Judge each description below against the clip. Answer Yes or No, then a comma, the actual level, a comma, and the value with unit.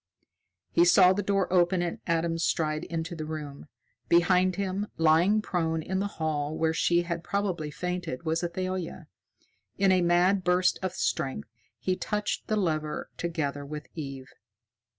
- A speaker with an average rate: Yes, average, 150 wpm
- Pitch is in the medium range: Yes, medium, 175 Hz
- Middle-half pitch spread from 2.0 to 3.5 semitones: Yes, average, 2.8 semitones